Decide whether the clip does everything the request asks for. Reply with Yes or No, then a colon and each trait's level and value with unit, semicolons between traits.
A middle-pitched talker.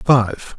No: low, 120 Hz